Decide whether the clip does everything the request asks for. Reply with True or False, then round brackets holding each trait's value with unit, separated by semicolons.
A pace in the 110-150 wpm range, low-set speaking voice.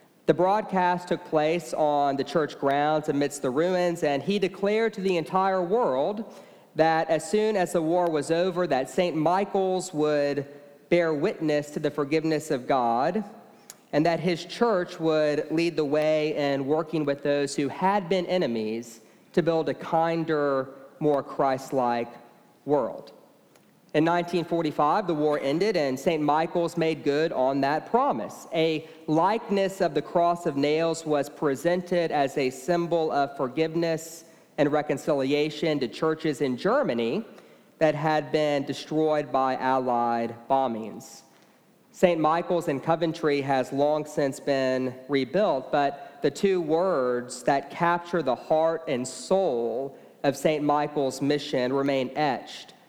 False (140 wpm; 155 Hz)